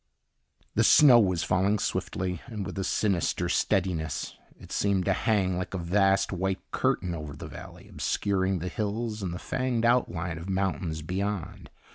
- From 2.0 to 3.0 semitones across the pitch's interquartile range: Yes, narrow, 2.5 semitones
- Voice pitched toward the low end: Yes, very low, 95 Hz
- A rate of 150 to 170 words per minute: Yes, average, 160 wpm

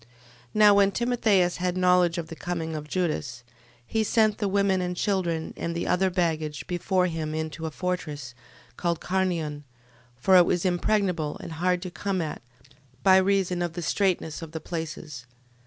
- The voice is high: No, medium, 175 Hz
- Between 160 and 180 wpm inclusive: Yes, average, 170 wpm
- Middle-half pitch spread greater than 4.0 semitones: No, average, 2.9 semitones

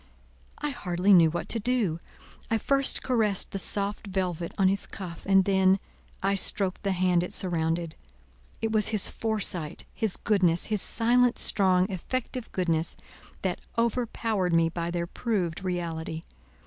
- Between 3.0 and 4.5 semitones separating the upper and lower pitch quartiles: Yes, average, 3.9 semitones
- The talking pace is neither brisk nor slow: Yes, average, 150 wpm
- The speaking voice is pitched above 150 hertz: Yes, high, 190 Hz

